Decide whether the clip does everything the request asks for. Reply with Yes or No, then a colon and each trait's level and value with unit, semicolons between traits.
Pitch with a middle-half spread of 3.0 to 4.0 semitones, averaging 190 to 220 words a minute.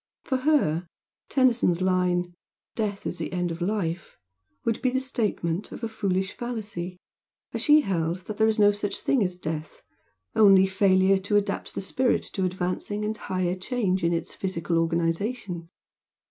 No: average, 3.6 semitones; average, 160 wpm